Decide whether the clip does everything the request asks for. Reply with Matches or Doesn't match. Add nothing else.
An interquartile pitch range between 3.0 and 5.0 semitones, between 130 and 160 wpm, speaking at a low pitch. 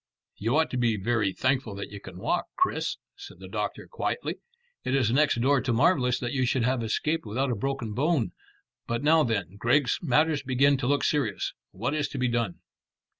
Doesn't match